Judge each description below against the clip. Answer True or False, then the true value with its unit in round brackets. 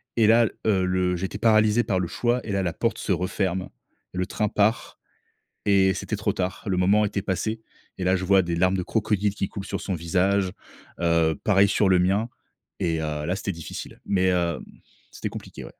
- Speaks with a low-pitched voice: True (95 Hz)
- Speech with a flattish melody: True (2.3 semitones)